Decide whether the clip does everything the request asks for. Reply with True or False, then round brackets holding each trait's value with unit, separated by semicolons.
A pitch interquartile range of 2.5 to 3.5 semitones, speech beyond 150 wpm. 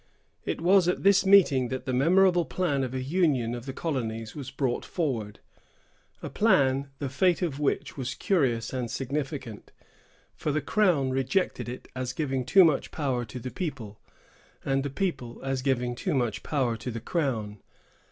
False (4.8 semitones; 170 wpm)